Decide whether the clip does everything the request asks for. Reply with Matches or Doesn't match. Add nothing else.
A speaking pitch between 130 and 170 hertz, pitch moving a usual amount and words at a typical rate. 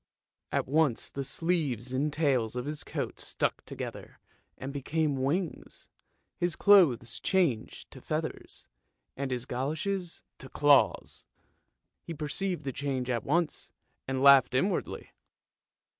Doesn't match